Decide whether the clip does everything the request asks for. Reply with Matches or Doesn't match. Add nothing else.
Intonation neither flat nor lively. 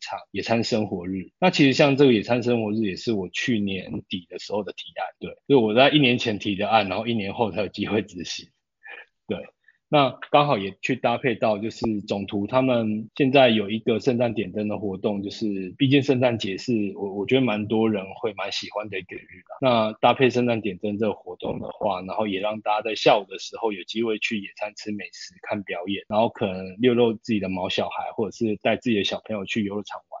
Matches